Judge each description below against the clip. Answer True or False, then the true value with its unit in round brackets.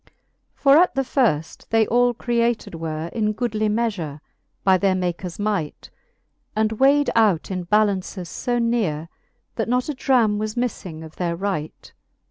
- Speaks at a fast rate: False (155 wpm)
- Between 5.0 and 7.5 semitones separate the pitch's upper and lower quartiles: True (5.3 semitones)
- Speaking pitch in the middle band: False (210 Hz)